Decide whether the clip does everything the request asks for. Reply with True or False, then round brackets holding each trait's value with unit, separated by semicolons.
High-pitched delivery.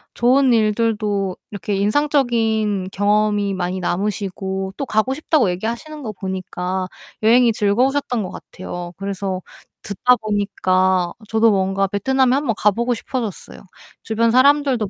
True (210 Hz)